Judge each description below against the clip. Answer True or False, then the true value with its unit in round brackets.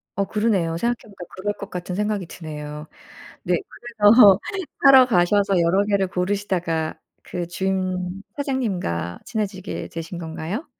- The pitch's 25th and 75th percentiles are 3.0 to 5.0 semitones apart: True (3.3 semitones)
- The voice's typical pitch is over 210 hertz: False (190 Hz)